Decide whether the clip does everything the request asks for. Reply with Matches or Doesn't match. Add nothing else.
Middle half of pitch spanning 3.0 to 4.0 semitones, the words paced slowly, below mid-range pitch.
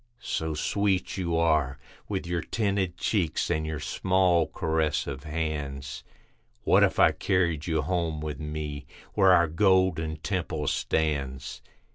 Matches